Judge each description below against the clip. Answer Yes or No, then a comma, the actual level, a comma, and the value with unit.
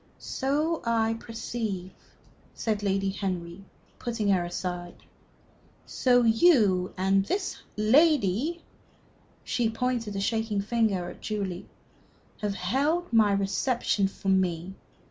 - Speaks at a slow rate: Yes, slow, 105 wpm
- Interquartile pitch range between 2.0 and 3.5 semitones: No, average, 3.9 semitones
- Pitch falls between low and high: No, high, 210 Hz